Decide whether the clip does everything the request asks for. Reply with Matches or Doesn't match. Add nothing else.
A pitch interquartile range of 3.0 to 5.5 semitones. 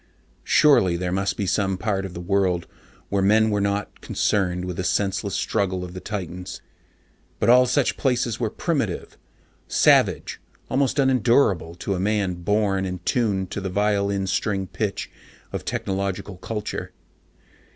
Doesn't match